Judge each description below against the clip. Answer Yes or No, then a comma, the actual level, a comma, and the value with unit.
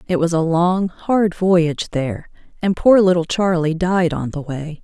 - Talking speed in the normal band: Yes, average, 185 wpm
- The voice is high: No, medium, 175 Hz